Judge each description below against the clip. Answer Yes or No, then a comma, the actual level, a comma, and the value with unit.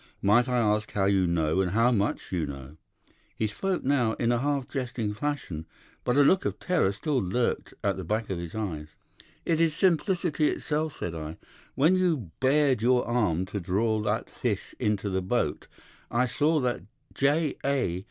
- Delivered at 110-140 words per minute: No, average, 180 wpm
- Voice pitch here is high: No, low, 115 Hz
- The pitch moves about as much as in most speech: No, wide, 6.9 semitones